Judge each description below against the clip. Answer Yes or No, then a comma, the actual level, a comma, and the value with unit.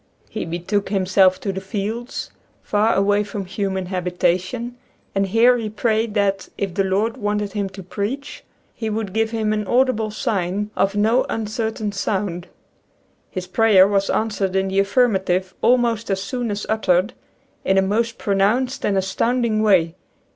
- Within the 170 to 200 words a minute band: No, average, 160 wpm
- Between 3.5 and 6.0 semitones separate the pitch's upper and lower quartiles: No, narrow, 2.6 semitones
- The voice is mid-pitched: No, high, 205 Hz